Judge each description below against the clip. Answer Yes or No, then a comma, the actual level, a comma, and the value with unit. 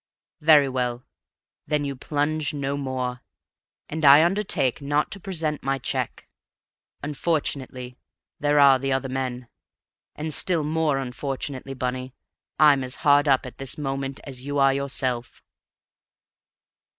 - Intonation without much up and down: Yes, narrow, 2.3 semitones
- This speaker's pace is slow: Yes, slow, 130 wpm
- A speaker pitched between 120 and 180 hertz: Yes, medium, 140 Hz